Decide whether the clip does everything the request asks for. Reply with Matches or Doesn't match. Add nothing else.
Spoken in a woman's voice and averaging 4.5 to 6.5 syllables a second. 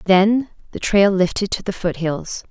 Doesn't match